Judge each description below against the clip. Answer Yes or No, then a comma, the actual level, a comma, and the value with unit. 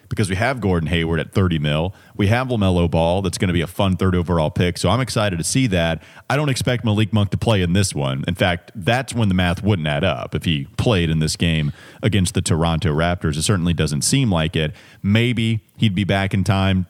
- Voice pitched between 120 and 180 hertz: No, very low, 95 Hz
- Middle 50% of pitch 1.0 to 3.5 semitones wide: No, average, 4.5 semitones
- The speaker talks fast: Yes, fast, 240 wpm